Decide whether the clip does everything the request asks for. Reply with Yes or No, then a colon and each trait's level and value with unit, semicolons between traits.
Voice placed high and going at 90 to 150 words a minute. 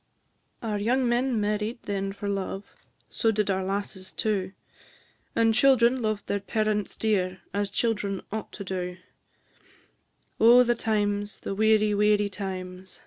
Yes: high, 205 Hz; average, 140 wpm